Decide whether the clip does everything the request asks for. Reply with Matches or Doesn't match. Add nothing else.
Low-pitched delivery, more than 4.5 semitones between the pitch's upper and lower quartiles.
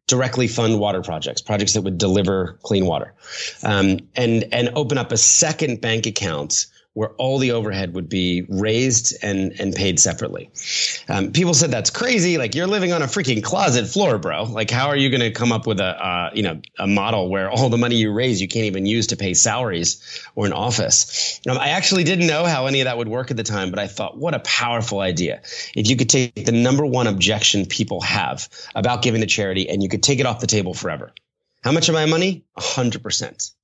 Matches